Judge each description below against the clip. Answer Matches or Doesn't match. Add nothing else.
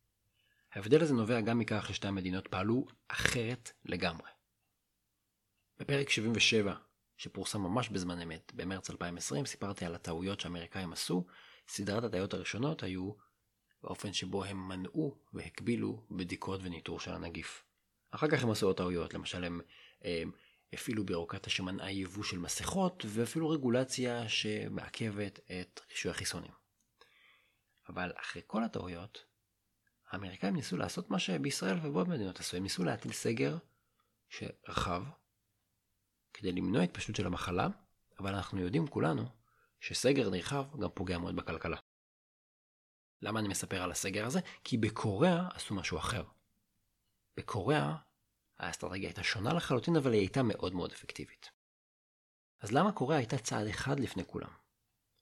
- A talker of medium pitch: Doesn't match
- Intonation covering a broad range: Doesn't match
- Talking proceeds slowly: Doesn't match